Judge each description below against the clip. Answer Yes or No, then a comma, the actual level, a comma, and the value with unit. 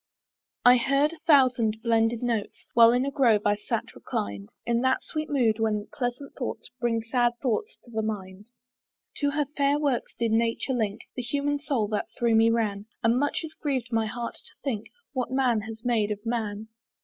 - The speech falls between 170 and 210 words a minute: Yes, average, 190 wpm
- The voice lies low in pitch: No, high, 235 Hz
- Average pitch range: Yes, average, 3.2 semitones